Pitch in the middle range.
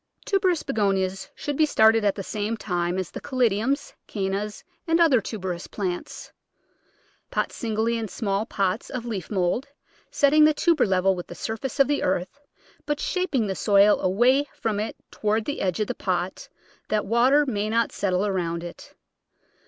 No: high, 215 Hz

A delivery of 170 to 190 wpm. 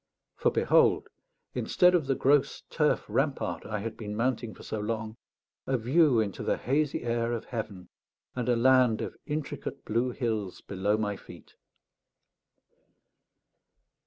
No: average, 140 wpm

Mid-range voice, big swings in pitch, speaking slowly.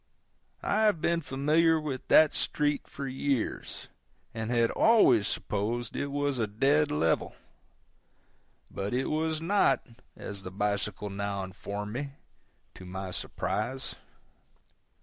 No: low, 125 Hz; wide, 6.5 semitones; slow, 125 wpm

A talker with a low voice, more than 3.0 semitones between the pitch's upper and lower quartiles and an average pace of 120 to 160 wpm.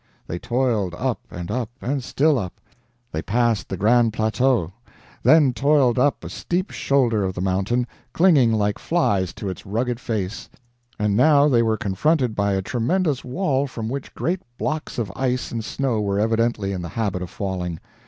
No: low, 115 Hz; average, 5.0 semitones; average, 175 wpm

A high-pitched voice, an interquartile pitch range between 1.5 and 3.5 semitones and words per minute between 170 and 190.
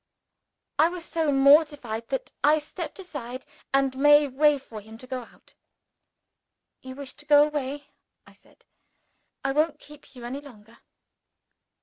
No: very high, 280 Hz; narrow, 2.6 semitones; average, 145 wpm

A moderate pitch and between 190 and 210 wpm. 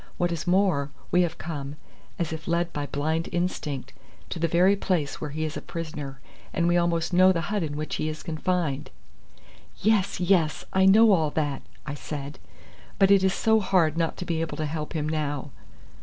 Yes: medium, 165 Hz; average, 200 wpm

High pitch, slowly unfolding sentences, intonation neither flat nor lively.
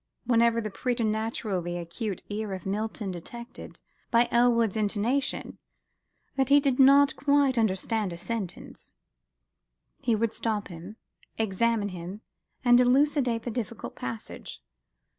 Yes: high, 225 Hz; slow, 120 wpm; average, 3.4 semitones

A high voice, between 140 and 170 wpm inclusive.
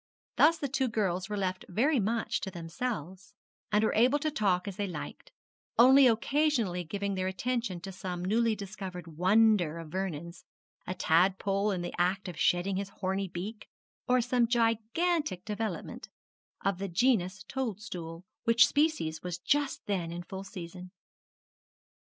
Yes: high, 195 Hz; average, 150 wpm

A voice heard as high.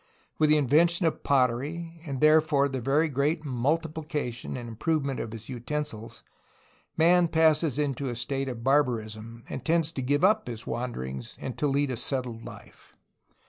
No: medium, 140 Hz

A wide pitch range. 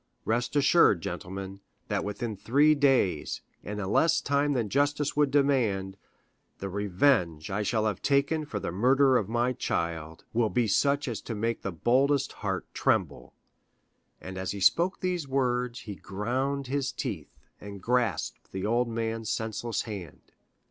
Yes: wide, 5.8 semitones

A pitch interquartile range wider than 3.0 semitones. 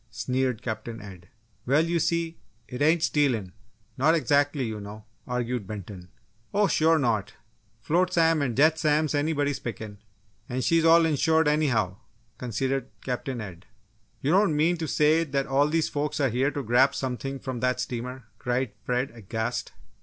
Yes: average, 4.7 semitones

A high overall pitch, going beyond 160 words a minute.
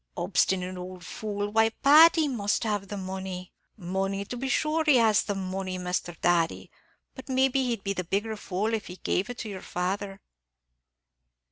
Yes: high, 200 Hz; average, 180 wpm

